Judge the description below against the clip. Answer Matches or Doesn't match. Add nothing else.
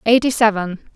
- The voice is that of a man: Doesn't match